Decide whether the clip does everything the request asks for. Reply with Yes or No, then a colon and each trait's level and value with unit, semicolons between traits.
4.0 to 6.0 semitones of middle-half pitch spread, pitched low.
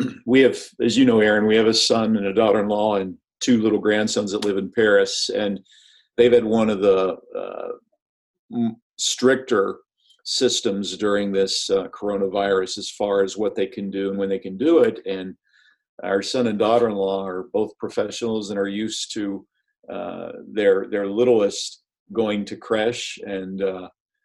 No: average, 3.3 semitones; low, 105 Hz